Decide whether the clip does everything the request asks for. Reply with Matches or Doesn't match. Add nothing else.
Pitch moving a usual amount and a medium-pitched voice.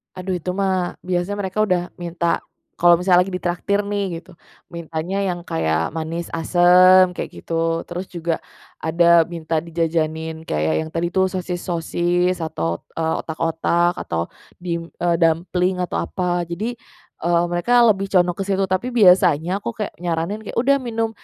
Doesn't match